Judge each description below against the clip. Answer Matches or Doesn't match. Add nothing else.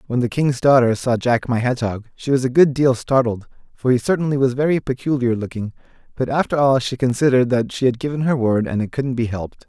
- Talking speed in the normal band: Doesn't match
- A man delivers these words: Matches